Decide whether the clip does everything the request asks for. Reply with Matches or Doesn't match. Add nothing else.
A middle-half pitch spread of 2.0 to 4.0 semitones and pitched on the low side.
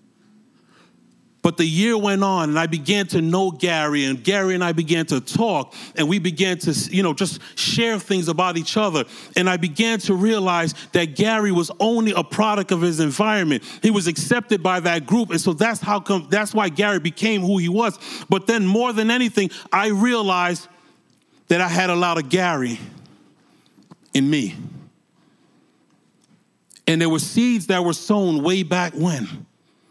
Doesn't match